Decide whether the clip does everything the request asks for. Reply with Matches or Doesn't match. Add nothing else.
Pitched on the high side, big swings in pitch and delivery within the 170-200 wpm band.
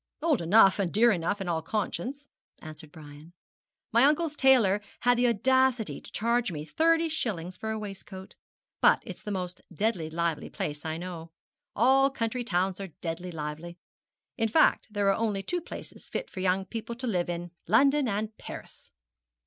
Matches